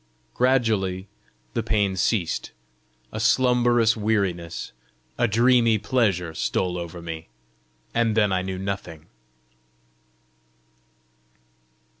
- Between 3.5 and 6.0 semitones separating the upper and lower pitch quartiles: Yes, average, 4.2 semitones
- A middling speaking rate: No, slow, 90 wpm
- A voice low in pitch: Yes, low, 105 Hz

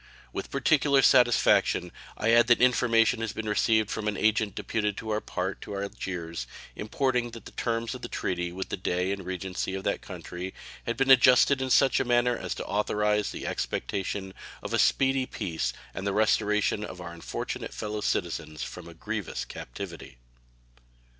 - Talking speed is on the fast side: No, average, 175 wpm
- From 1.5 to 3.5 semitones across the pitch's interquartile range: No, average, 3.9 semitones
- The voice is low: Yes, low, 105 Hz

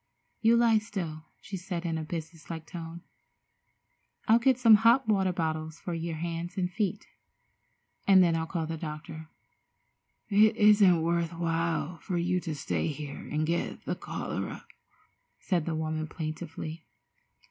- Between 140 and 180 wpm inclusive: Yes, average, 150 wpm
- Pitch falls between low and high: Yes, medium, 170 Hz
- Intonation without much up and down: No, average, 3.2 semitones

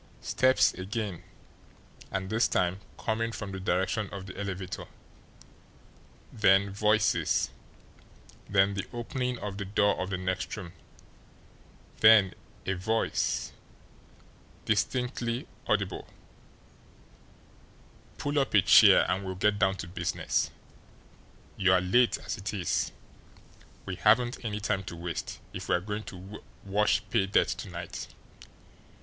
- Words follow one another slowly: Yes, slow, 120 wpm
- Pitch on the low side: Yes, low, 100 Hz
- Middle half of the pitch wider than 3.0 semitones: No, narrow, 2.5 semitones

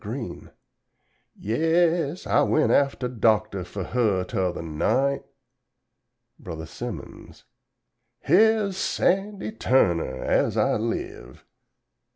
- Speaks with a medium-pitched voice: No, low, 125 Hz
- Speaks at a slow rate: Yes, slow, 95 wpm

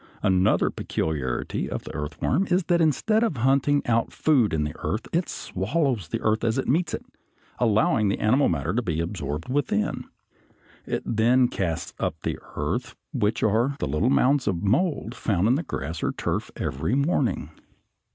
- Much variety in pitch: Yes, wide, 7.8 semitones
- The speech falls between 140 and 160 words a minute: No, average, 170 wpm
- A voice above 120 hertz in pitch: No, low, 115 Hz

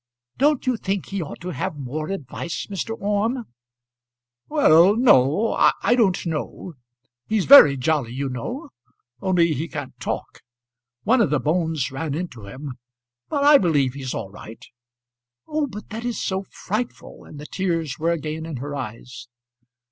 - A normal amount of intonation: No, wide, 7.0 semitones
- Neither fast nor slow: Yes, average, 155 wpm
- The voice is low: No, medium, 165 Hz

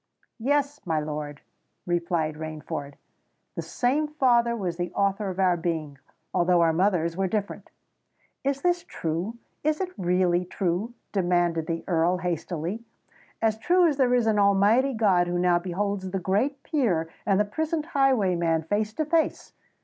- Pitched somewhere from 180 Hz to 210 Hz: Yes, high, 190 Hz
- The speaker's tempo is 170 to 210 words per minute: No, average, 145 wpm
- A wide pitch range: Yes, wide, 5.8 semitones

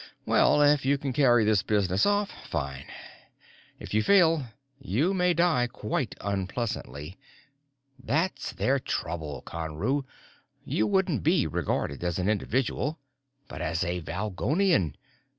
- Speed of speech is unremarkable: No, slow, 125 wpm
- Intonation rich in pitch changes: Yes, wide, 8.4 semitones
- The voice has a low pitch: Yes, low, 110 Hz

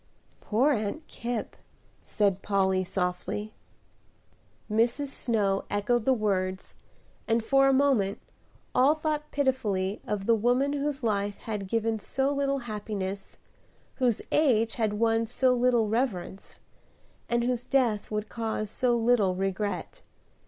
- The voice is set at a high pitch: Yes, high, 225 Hz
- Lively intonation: No, average, 3.9 semitones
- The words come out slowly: Yes, slow, 125 wpm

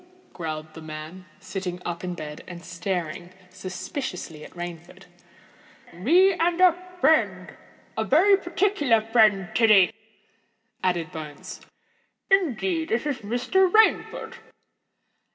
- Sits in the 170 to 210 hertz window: Yes, high, 190 Hz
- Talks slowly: Yes, slow, 100 wpm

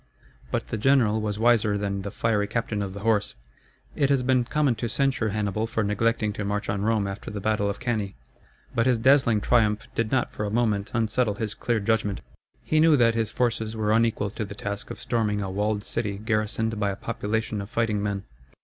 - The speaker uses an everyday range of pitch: No, narrow, 2.1 semitones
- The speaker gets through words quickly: Yes, fast, 210 wpm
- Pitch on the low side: Yes, low, 110 Hz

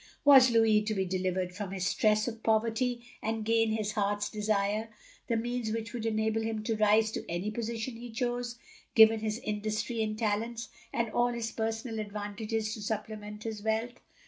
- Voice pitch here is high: Yes, high, 220 Hz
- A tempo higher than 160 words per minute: Yes, average, 185 wpm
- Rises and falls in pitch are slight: Yes, narrow, 1.3 semitones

